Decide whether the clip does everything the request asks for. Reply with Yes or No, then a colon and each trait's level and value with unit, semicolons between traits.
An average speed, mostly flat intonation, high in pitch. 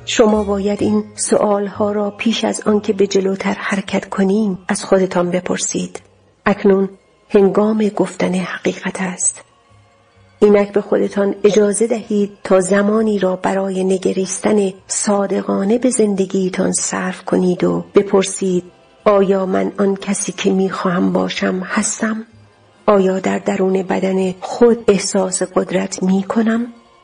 Yes: average, 125 wpm; narrow, 1.8 semitones; high, 195 Hz